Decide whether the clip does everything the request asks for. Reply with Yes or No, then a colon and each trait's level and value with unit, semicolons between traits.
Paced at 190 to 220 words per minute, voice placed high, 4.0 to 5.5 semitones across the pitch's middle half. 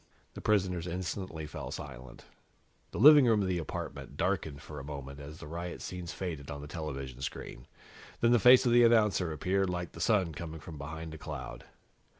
No: average, 195 wpm; very low, 85 Hz; average, 4.6 semitones